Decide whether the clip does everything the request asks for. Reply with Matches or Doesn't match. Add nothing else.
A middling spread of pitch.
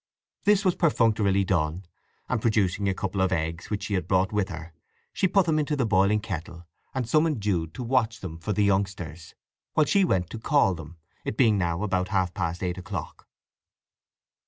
Matches